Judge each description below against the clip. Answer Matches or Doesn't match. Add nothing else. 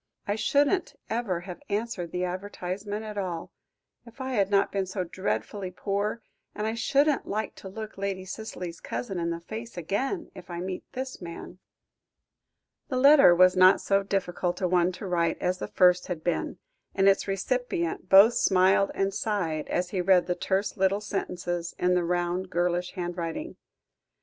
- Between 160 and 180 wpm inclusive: Matches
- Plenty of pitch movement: Doesn't match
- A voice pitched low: Doesn't match